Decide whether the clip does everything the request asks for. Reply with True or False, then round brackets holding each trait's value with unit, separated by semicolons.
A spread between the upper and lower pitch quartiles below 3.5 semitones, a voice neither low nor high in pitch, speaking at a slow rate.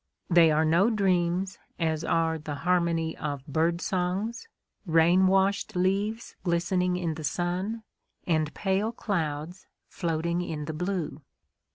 True (3.0 semitones; 175 Hz; 130 wpm)